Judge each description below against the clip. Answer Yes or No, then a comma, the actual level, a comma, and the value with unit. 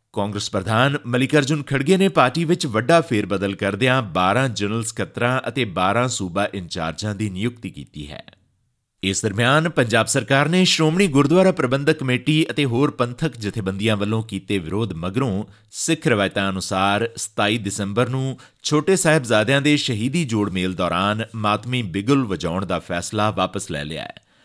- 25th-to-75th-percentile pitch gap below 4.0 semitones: No, wide, 5.5 semitones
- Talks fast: No, average, 150 wpm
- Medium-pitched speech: No, low, 115 Hz